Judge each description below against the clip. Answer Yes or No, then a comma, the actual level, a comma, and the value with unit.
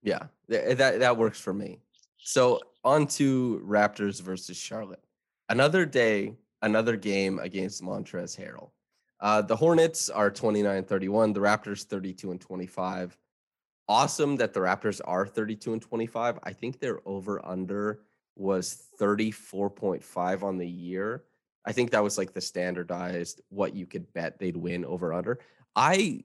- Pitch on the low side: Yes, low, 100 Hz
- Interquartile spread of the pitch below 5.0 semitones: Yes, average, 3.2 semitones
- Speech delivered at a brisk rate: No, average, 145 wpm